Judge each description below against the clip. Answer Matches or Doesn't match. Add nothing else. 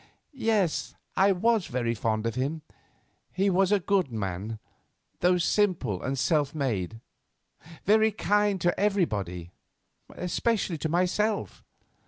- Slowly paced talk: Matches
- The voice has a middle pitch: Matches